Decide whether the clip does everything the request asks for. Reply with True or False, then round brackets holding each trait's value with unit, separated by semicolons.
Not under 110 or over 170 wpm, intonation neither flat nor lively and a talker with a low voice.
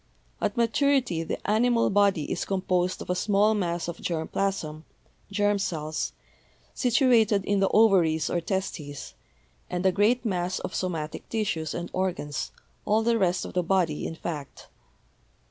False (150 wpm; 3.8 semitones; 190 Hz)